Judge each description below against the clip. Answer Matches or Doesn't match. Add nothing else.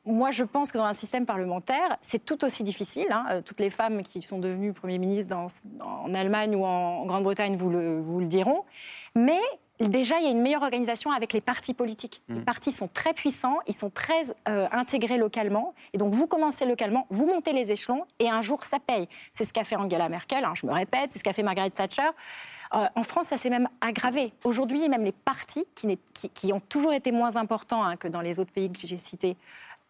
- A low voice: Doesn't match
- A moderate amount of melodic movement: Doesn't match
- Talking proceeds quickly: Matches